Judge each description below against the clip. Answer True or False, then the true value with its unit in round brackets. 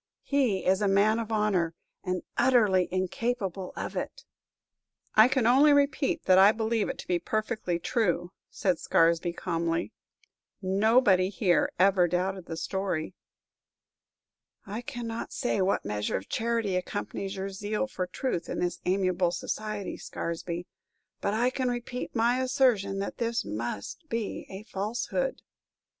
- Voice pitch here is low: False (200 Hz)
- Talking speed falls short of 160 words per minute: True (140 wpm)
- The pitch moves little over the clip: False (4.2 semitones)